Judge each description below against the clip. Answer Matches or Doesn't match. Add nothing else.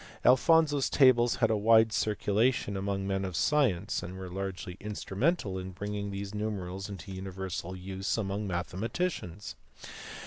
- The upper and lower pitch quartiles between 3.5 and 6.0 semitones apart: Doesn't match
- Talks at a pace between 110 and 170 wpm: Matches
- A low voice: Matches